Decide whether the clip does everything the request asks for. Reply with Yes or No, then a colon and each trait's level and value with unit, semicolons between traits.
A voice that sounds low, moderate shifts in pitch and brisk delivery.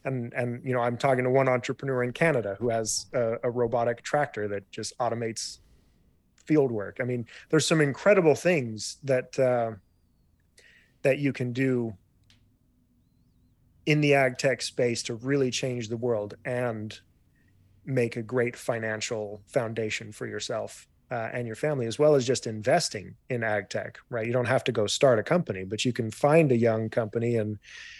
No: low, 120 Hz; average, 3.2 semitones; average, 175 wpm